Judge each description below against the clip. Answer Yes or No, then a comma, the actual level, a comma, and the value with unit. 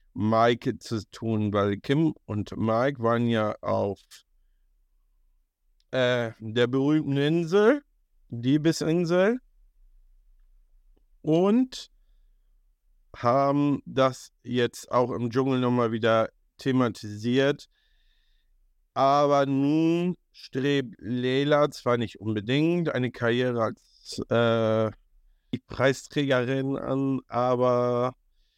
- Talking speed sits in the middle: No, slow, 85 wpm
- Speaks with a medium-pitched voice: No, low, 125 Hz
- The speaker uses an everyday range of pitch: Yes, average, 4.4 semitones